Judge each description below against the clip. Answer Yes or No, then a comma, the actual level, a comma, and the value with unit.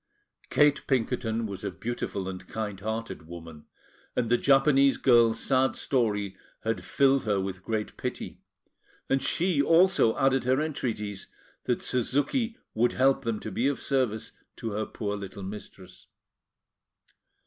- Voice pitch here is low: Yes, low, 115 Hz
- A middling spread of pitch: Yes, average, 4.7 semitones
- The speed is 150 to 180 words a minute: No, average, 140 wpm